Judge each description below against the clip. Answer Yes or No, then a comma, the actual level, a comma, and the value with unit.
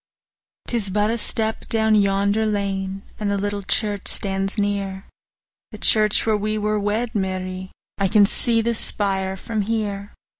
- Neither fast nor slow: Yes, average, 150 wpm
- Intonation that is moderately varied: No, narrow, 1.7 semitones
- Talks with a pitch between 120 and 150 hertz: No, high, 205 Hz